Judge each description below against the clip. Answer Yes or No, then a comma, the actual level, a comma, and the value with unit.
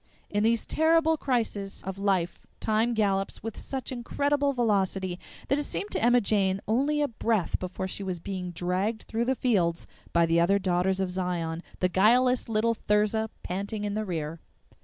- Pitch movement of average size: Yes, average, 4.1 semitones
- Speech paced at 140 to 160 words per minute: No, average, 175 wpm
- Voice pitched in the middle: No, high, 205 Hz